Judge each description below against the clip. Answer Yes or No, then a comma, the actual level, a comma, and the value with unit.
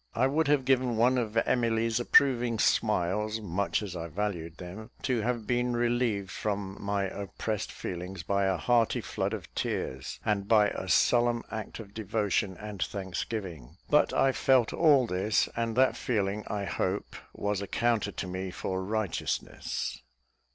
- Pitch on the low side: Yes, low, 105 Hz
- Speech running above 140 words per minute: Yes, average, 155 wpm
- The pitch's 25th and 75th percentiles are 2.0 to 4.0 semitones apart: Yes, average, 3.7 semitones